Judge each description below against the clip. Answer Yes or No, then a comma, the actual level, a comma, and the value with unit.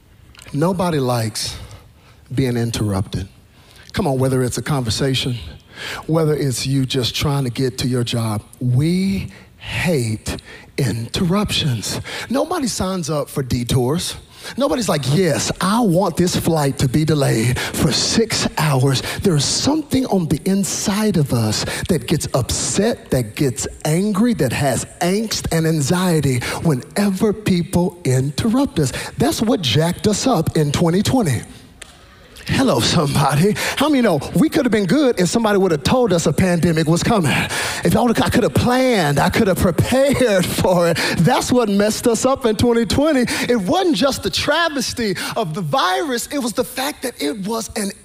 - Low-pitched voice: No, medium, 165 Hz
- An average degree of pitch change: No, wide, 8.8 semitones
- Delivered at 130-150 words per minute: No, average, 160 wpm